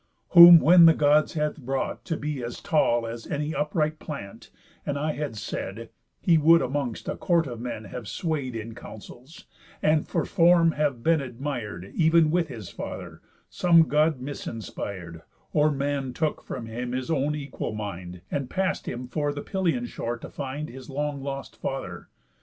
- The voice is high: No, medium, 140 Hz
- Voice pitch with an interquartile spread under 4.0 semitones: No, average, 4.5 semitones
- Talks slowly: No, average, 170 wpm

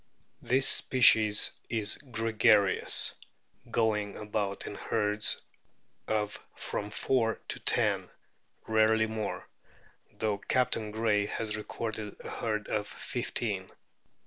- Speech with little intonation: Yes, narrow, 1.2 semitones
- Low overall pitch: Yes, low, 110 Hz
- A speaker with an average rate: No, slow, 100 wpm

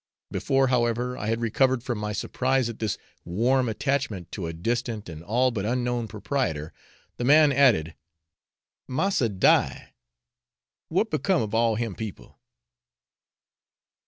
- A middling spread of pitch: Yes, average, 3.7 semitones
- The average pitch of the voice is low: Yes, low, 120 Hz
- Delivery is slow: Yes, slow, 130 wpm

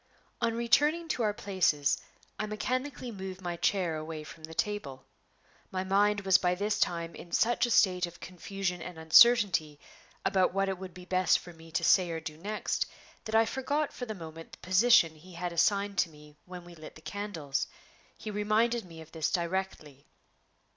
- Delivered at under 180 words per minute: No, average, 190 wpm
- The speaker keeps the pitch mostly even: No, average, 4.1 semitones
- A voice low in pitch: No, medium, 185 Hz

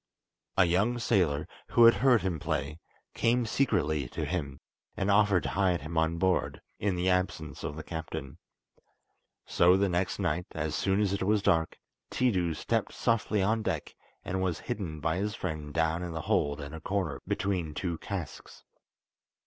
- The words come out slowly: No, average, 175 wpm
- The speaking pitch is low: Yes, very low, 90 Hz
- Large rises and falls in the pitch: No, average, 4.1 semitones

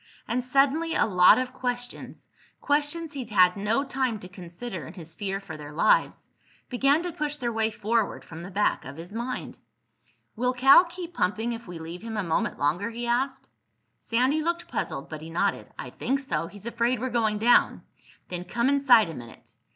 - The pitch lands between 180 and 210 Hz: No, high, 230 Hz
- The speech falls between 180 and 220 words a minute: Yes, average, 185 wpm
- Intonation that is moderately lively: No, wide, 6.5 semitones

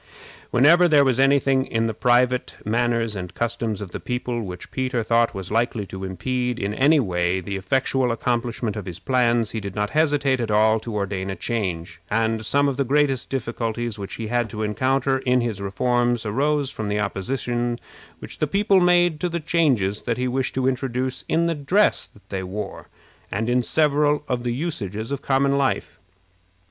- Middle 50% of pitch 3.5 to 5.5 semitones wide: Yes, average, 4.1 semitones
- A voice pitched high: No, low, 120 Hz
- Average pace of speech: Yes, average, 190 wpm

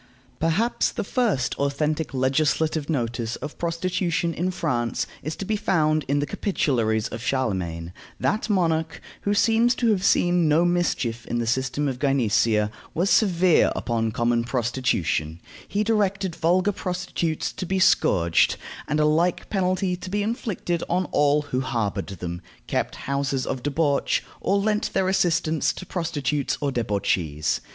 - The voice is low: No, medium, 155 Hz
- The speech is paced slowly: No, average, 150 wpm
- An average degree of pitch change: No, wide, 6.9 semitones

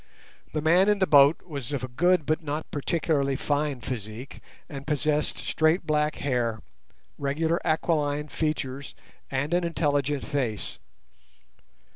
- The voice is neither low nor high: Yes, medium, 150 Hz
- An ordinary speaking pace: No, slow, 130 wpm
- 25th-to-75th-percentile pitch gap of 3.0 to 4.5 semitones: No, narrow, 2.4 semitones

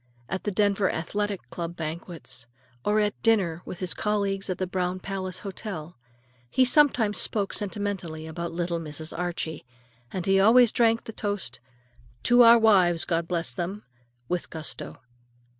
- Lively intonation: No, average, 3.5 semitones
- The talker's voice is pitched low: No, high, 190 Hz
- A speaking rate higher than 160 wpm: No, average, 150 wpm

